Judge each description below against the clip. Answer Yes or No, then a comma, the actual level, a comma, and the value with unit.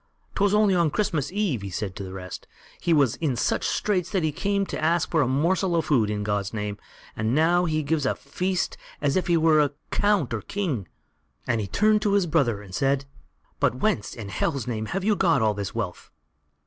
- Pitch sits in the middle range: Yes, medium, 150 Hz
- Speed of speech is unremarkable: No, fast, 215 wpm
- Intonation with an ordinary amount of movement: No, wide, 8.6 semitones